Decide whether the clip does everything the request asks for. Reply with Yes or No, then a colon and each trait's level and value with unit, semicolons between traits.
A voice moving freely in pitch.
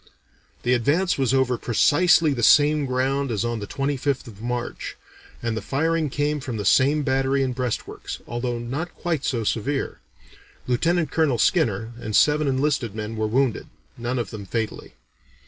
No: average, 3.6 semitones